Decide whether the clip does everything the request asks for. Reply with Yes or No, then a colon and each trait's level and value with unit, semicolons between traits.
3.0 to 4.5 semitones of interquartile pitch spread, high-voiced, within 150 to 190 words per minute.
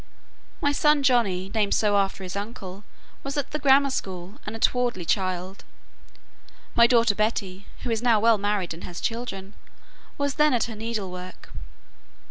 Yes: average, 4.2 semitones; high, 215 Hz; average, 160 wpm